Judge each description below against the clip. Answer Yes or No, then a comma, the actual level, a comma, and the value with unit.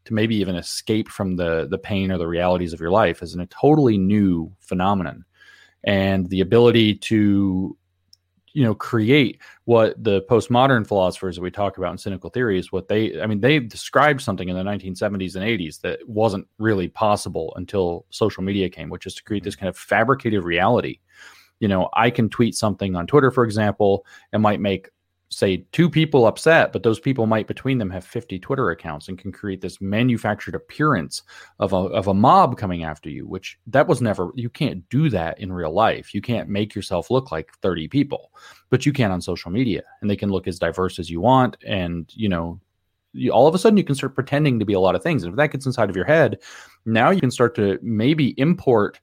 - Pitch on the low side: Yes, low, 100 Hz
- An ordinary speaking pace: No, fast, 215 wpm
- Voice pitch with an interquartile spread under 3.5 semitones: No, average, 3.9 semitones